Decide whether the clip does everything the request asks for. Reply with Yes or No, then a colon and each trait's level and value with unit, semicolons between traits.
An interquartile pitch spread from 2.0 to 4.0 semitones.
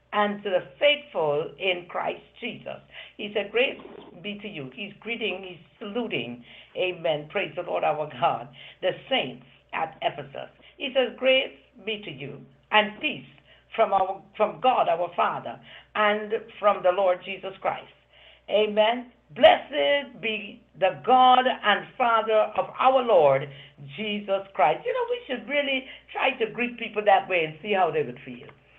No: average, 4.9 semitones